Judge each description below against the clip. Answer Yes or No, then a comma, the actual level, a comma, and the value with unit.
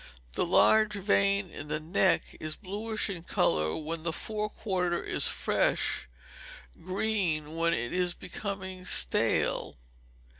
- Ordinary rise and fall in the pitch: Yes, average, 3.8 semitones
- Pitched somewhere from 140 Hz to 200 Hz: Yes, medium, 185 Hz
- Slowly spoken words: Yes, slow, 125 wpm